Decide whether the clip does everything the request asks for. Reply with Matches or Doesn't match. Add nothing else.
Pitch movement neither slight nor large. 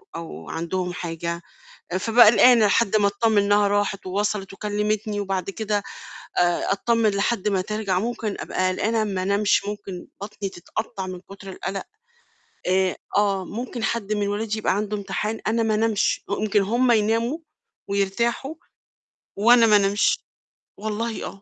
Doesn't match